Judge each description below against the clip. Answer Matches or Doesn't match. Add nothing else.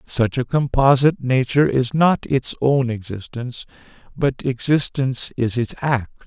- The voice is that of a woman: Doesn't match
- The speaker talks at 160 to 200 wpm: Doesn't match